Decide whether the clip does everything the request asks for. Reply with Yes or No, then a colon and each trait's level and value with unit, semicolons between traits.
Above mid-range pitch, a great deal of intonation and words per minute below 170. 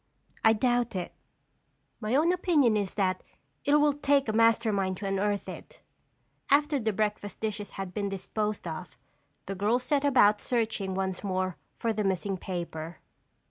No: high, 210 Hz; average, 4.1 semitones; average, 160 wpm